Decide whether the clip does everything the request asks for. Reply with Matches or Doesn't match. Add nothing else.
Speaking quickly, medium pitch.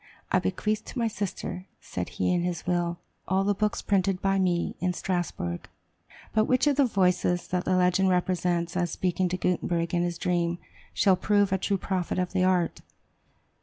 Doesn't match